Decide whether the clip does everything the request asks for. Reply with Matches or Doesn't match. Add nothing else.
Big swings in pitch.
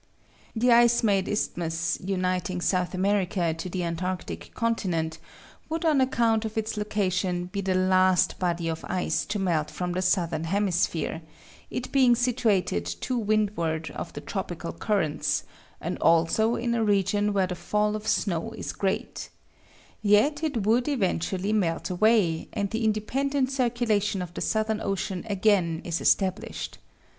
Doesn't match